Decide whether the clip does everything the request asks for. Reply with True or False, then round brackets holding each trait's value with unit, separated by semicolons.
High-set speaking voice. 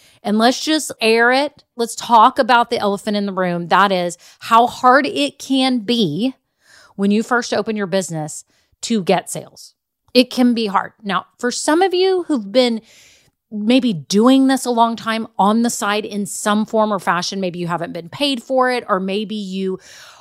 True (225 Hz)